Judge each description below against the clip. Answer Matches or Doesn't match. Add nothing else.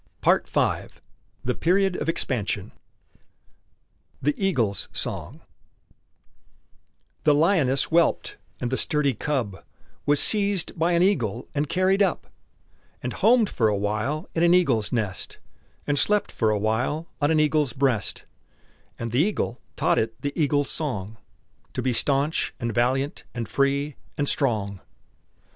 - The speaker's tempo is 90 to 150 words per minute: Matches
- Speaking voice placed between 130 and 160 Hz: Matches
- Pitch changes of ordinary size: Doesn't match